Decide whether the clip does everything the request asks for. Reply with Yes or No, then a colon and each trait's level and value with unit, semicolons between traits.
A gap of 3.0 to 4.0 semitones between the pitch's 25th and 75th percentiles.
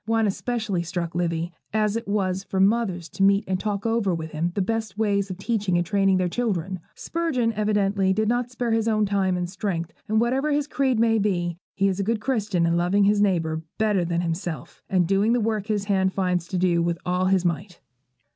Yes: average, 3.6 semitones